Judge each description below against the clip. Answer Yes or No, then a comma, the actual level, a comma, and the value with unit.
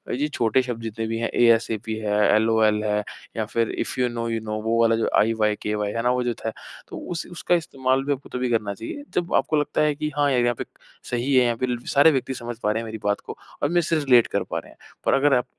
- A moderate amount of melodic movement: Yes, average, 3.2 semitones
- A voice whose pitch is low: Yes, low, 120 Hz